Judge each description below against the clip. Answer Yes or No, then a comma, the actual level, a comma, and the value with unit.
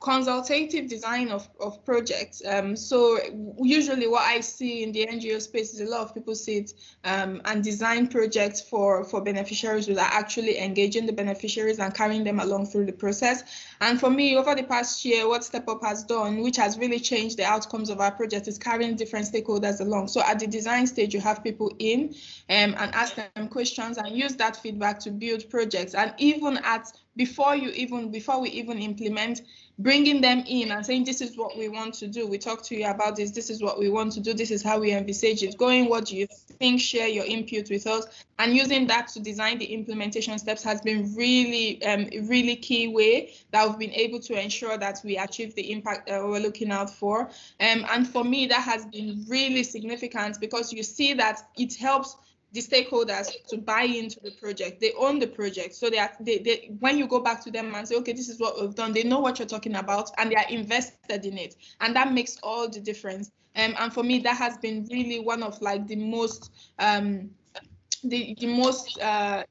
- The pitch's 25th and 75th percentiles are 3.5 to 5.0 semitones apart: No, narrow, 2.4 semitones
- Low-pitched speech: No, high, 225 Hz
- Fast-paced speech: Yes, fast, 215 wpm